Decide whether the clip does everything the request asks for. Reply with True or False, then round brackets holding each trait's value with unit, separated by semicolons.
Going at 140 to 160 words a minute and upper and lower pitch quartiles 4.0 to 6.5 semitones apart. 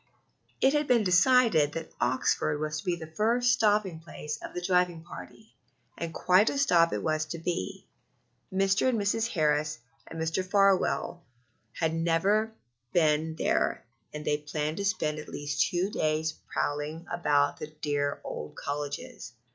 True (155 wpm; 4.5 semitones)